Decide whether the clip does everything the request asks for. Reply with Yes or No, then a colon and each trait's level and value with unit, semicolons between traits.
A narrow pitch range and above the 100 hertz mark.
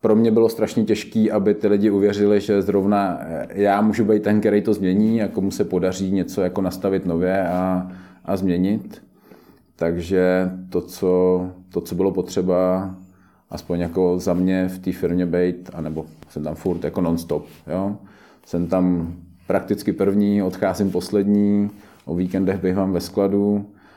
No: narrow, 2.2 semitones; very low, 95 Hz